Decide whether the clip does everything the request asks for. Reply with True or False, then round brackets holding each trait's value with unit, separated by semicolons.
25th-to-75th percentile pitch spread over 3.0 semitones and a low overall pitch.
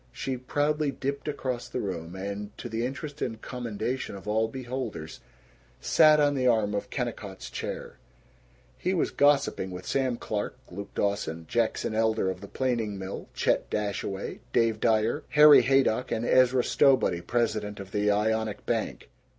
True (4.2 semitones; 115 Hz)